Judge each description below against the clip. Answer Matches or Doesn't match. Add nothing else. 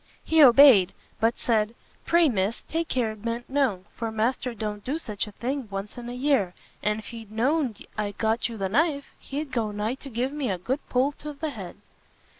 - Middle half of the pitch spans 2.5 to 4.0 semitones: Doesn't match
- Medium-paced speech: Doesn't match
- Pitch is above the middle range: Matches